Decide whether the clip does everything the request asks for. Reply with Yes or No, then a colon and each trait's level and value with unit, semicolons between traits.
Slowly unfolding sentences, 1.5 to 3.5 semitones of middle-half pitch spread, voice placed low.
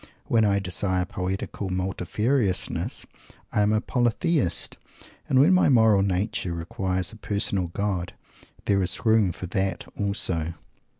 Yes: slow, 130 wpm; average, 3.1 semitones; low, 100 Hz